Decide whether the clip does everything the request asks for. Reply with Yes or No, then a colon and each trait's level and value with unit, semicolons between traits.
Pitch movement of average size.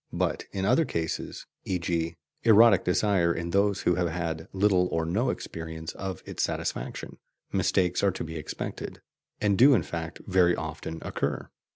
Yes: average, 3.3 semitones